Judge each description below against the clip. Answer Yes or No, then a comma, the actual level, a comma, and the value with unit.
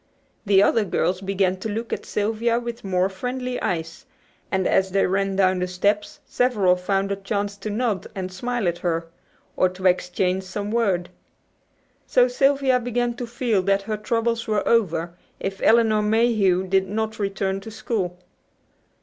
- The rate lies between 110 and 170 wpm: Yes, average, 165 wpm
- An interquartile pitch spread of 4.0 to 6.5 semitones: No, average, 3.5 semitones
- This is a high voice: Yes, high, 200 Hz